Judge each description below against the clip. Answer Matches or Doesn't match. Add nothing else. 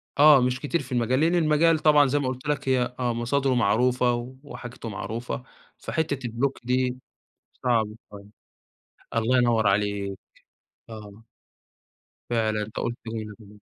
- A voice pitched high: Doesn't match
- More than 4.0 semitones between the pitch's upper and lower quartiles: Doesn't match